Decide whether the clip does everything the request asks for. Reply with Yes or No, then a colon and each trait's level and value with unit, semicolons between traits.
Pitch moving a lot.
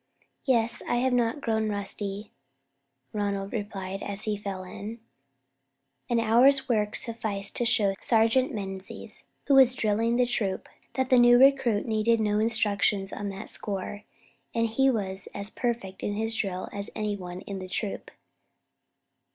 No: average, 3.0 semitones